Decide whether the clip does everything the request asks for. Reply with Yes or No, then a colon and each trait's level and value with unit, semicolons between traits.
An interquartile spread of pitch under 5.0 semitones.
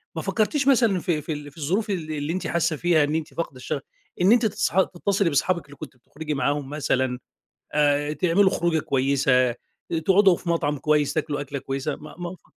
Yes: average, 3.9 semitones